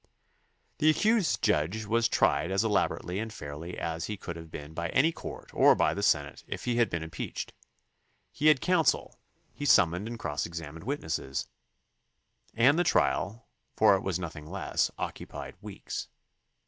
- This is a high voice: No, very low, 95 Hz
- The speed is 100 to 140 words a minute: No, average, 165 wpm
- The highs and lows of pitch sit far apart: Yes, wide, 6.4 semitones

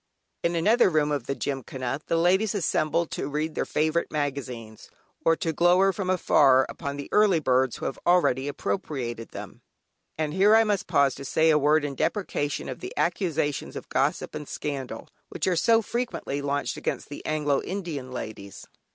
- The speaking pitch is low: No, medium, 150 Hz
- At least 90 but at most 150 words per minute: No, average, 175 wpm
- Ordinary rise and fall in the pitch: Yes, average, 4.3 semitones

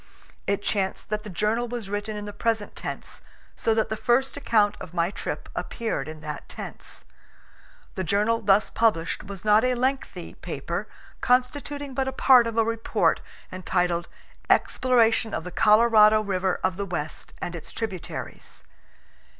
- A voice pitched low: No, high, 215 Hz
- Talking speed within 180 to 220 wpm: No, average, 160 wpm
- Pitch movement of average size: Yes, average, 3.5 semitones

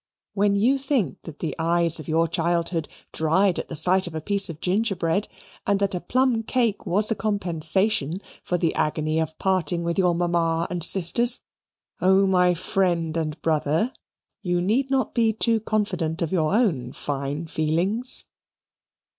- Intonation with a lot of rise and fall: No, average, 3.8 semitones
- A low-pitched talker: No, medium, 175 Hz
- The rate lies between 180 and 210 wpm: No, average, 165 wpm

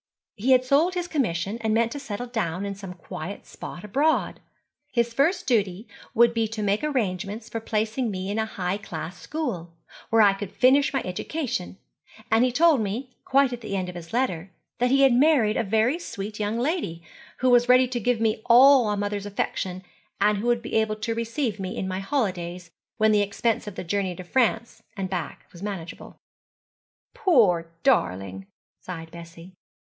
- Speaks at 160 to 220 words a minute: Yes, average, 190 wpm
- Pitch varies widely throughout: No, average, 4.8 semitones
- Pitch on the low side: No, high, 215 Hz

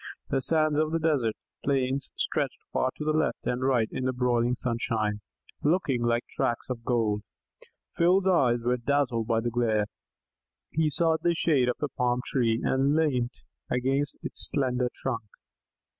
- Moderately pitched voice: No, low, 125 Hz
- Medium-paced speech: Yes, average, 160 wpm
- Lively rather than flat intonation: No, average, 3.7 semitones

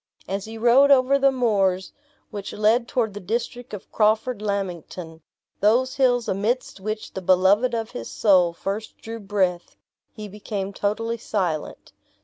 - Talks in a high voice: Yes, high, 210 Hz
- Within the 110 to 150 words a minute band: Yes, average, 145 wpm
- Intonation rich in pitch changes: No, average, 3.4 semitones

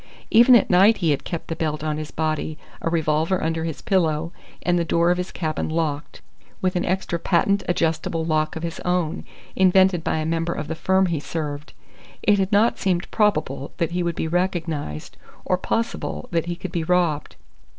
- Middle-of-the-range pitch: Yes, medium, 170 Hz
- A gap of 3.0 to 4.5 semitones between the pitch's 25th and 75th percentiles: No, narrow, 2.5 semitones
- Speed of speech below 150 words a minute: No, average, 195 wpm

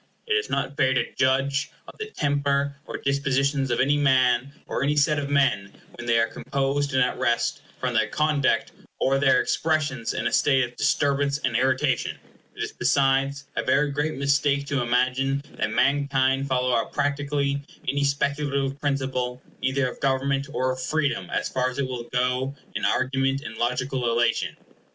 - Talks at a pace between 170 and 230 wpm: Yes, average, 175 wpm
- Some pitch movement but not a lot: No, narrow, 1.7 semitones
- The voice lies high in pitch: No, low, 135 Hz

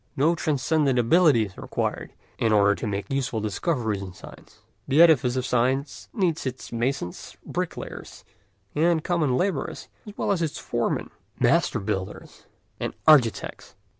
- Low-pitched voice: Yes, low, 130 Hz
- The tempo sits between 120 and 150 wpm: Yes, average, 140 wpm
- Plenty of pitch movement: Yes, wide, 6.1 semitones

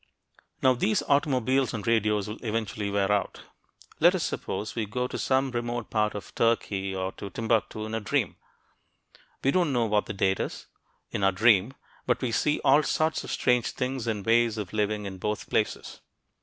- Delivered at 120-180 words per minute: No, average, 190 wpm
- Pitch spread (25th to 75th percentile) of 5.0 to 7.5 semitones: No, average, 3.5 semitones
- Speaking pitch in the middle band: No, low, 115 Hz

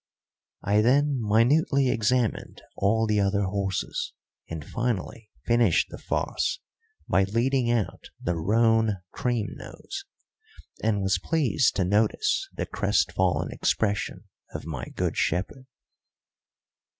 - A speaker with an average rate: No, slow, 115 wpm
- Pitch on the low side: Yes, low, 110 Hz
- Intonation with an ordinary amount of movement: Yes, average, 3.5 semitones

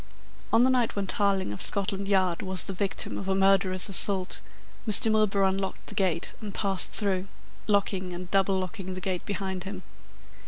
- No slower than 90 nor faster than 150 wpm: No, average, 180 wpm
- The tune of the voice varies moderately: No, narrow, 1.3 semitones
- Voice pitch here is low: No, high, 195 Hz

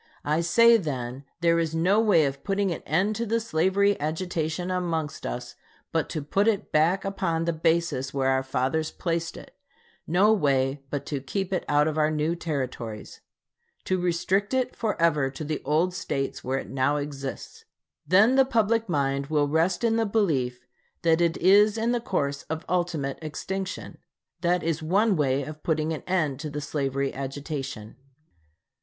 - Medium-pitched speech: Yes, medium, 160 Hz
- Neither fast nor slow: Yes, average, 175 wpm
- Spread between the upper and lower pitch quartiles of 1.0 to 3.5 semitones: No, average, 4.9 semitones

